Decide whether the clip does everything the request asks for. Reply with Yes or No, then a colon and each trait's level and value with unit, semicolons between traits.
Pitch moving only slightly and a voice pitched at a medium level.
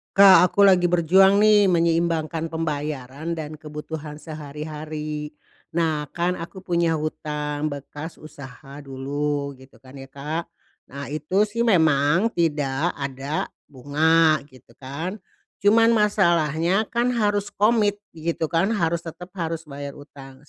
No: average, 3.4 semitones; medium, 160 Hz